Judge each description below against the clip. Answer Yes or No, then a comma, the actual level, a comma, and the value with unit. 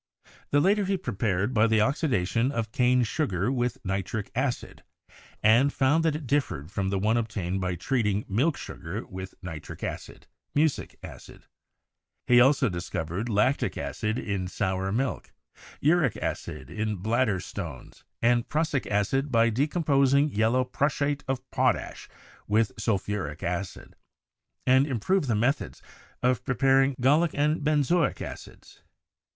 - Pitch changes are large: Yes, wide, 5.8 semitones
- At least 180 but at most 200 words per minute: No, average, 140 wpm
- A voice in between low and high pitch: No, low, 120 Hz